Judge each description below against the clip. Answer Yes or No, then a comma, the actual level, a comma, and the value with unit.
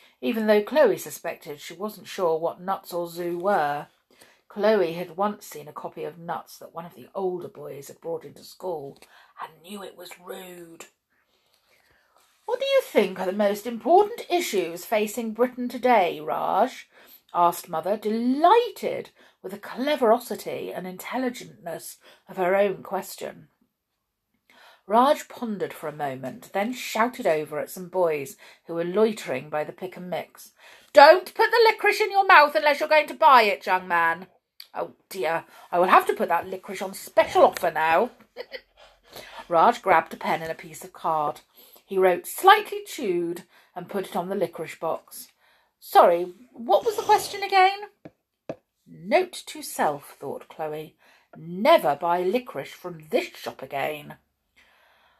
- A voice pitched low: No, high, 205 Hz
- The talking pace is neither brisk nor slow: Yes, average, 160 wpm